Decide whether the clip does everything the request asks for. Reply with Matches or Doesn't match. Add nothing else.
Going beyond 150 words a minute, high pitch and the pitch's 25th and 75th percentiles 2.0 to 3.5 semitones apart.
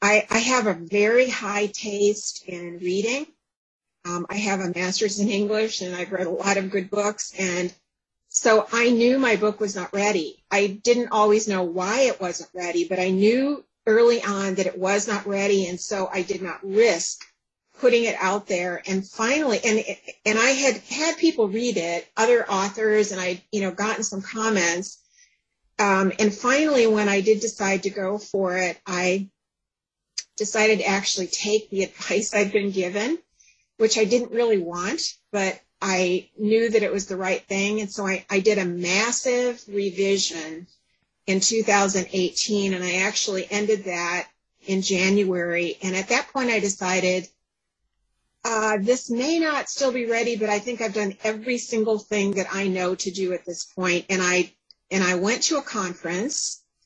Matches